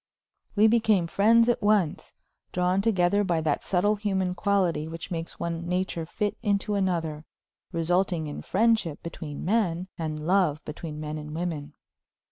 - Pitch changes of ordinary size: Yes, average, 3.9 semitones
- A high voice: No, medium, 180 Hz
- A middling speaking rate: Yes, average, 145 wpm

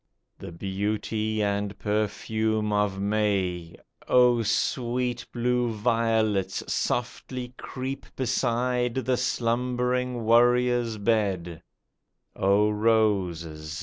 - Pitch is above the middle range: No, low, 110 Hz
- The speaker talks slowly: Yes, slow, 80 wpm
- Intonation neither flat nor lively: Yes, average, 3.3 semitones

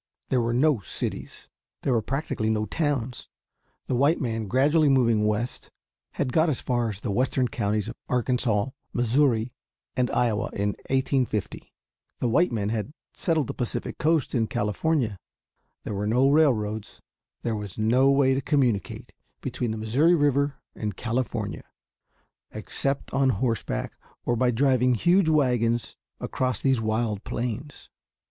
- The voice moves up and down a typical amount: Yes, average, 3.8 semitones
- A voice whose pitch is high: No, low, 125 Hz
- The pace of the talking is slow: No, average, 145 wpm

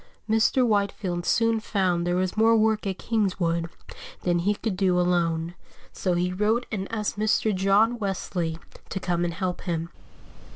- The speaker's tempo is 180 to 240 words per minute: No, average, 160 wpm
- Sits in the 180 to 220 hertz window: Yes, high, 190 Hz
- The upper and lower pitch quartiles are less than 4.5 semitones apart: Yes, average, 3.6 semitones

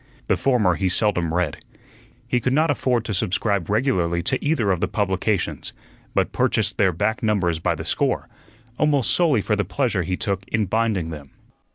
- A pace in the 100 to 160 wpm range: No, average, 180 wpm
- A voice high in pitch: No, low, 105 Hz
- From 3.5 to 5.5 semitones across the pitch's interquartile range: Yes, average, 4.8 semitones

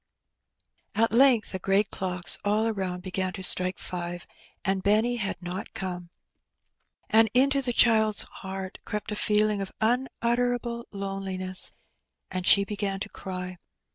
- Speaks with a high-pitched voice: Yes, high, 200 Hz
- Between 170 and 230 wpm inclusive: No, average, 140 wpm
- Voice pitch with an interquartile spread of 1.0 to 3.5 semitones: Yes, average, 3.1 semitones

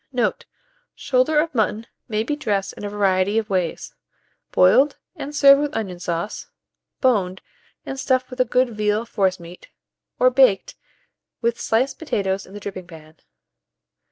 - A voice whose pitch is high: Yes, high, 215 Hz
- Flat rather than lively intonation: No, average, 5.1 semitones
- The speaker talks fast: No, average, 150 wpm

